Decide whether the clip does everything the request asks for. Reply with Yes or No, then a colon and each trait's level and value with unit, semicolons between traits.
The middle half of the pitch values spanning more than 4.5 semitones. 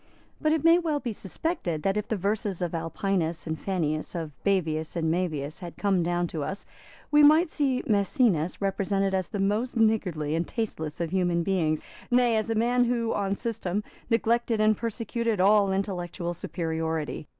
Yes: average, 5.0 semitones